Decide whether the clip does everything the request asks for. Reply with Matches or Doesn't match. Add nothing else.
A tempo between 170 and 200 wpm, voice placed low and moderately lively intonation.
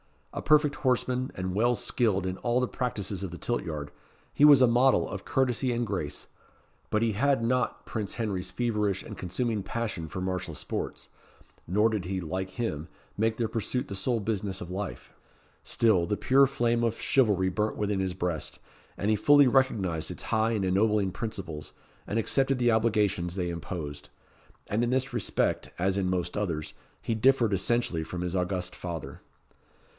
Matches